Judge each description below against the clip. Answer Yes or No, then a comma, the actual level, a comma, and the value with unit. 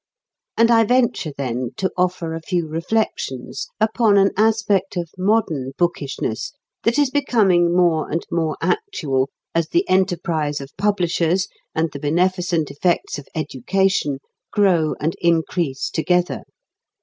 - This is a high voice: No, medium, 175 Hz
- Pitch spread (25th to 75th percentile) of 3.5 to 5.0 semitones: Yes, average, 4.3 semitones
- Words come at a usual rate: No, slow, 130 wpm